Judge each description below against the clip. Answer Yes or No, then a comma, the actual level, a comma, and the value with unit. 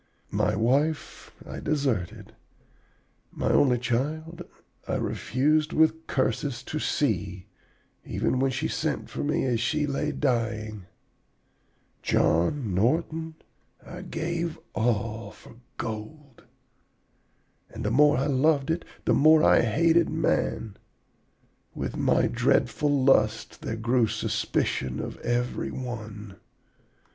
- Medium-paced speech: No, slow, 115 wpm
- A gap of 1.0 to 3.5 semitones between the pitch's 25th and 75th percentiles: No, wide, 5.5 semitones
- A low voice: Yes, low, 130 Hz